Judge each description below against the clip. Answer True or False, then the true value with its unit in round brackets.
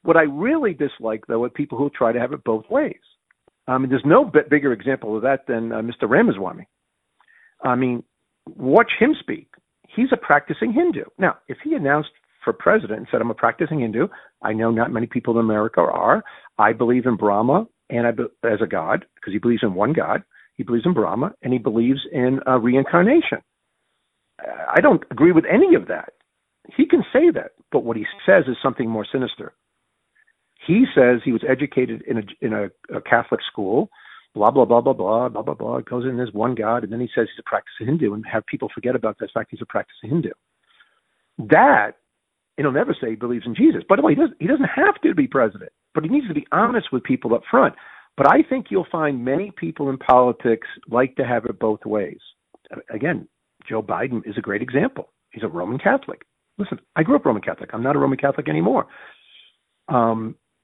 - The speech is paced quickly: True (210 wpm)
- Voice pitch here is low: True (130 Hz)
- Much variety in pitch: True (6.8 semitones)